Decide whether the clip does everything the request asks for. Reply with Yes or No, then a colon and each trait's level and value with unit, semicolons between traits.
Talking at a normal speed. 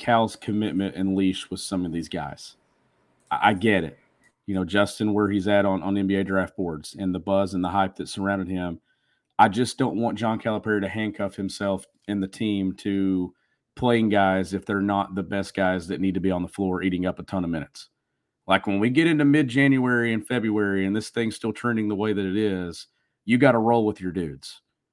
No: fast, 220 wpm